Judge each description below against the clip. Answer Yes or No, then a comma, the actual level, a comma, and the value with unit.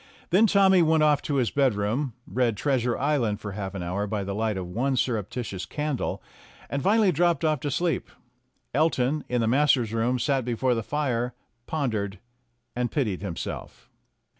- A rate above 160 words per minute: Yes, average, 175 wpm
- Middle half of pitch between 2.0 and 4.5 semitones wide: No, wide, 5.4 semitones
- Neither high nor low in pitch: No, low, 125 Hz